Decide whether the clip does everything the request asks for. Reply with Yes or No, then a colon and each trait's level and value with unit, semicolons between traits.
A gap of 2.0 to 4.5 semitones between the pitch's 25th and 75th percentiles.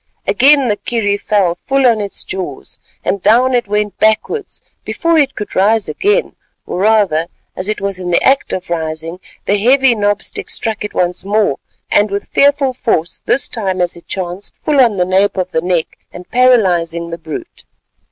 No: average, 5.0 semitones